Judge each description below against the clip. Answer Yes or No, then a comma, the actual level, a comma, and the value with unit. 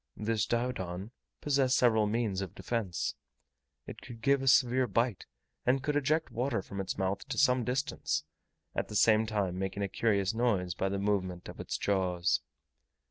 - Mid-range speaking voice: No, low, 110 Hz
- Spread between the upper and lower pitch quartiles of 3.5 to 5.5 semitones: Yes, average, 4.6 semitones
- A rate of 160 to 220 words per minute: Yes, average, 170 wpm